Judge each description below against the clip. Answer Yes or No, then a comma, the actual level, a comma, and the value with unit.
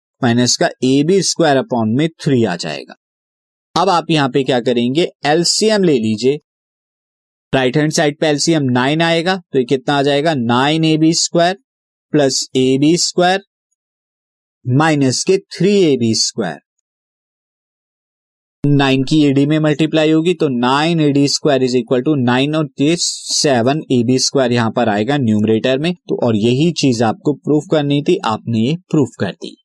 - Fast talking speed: No, average, 165 wpm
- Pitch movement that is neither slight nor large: Yes, average, 4.2 semitones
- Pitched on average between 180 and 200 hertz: No, medium, 140 Hz